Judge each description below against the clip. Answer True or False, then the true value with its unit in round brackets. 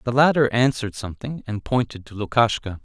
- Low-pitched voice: True (115 Hz)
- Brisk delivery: False (170 wpm)